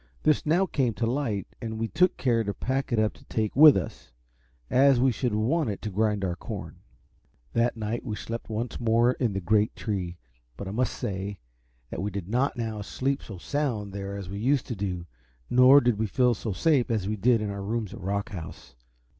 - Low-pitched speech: Yes, low, 110 Hz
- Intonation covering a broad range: No, average, 3.8 semitones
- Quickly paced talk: Yes, fast, 215 wpm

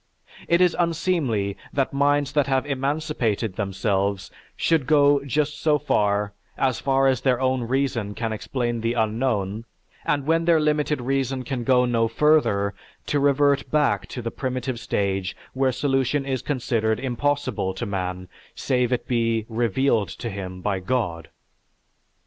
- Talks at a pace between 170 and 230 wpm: No, average, 150 wpm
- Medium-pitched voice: No, low, 130 Hz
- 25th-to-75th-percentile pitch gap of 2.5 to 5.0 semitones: Yes, average, 4.5 semitones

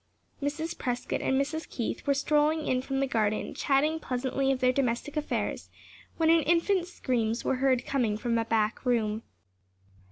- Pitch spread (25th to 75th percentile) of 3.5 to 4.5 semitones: Yes, average, 3.8 semitones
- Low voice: No, very high, 270 Hz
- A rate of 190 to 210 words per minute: No, average, 165 wpm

